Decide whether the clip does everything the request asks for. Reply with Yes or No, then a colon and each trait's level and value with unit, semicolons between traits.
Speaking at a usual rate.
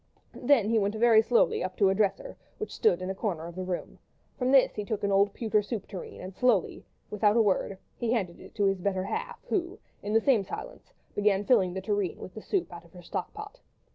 No: fast, 240 wpm